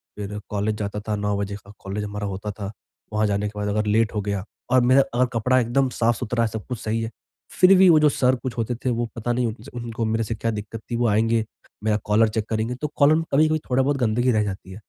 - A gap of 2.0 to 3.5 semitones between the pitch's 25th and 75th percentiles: Yes, average, 3.0 semitones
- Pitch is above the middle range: No, low, 115 Hz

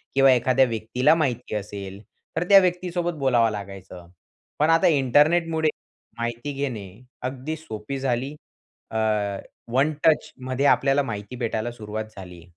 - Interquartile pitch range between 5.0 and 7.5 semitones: Yes, average, 5.3 semitones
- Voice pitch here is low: Yes, low, 130 Hz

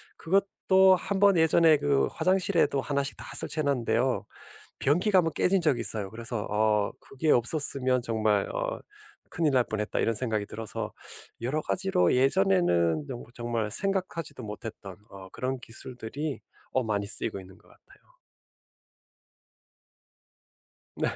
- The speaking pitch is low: Yes, low, 130 Hz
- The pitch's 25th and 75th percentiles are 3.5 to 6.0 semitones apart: No, wide, 6.7 semitones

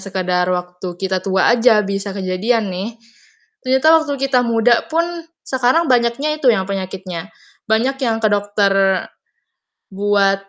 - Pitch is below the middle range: No, high, 210 Hz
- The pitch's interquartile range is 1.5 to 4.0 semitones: No, average, 4.5 semitones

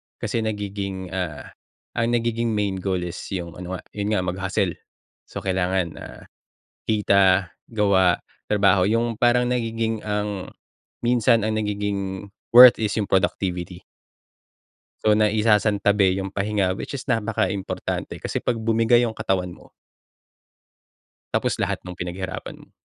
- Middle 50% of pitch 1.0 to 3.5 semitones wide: Yes, average, 3.0 semitones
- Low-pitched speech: Yes, low, 100 Hz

